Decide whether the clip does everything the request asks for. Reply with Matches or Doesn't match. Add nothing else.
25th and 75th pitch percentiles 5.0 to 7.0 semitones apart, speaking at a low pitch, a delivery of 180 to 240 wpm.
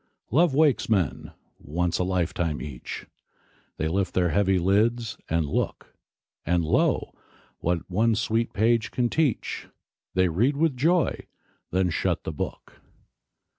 Doesn't match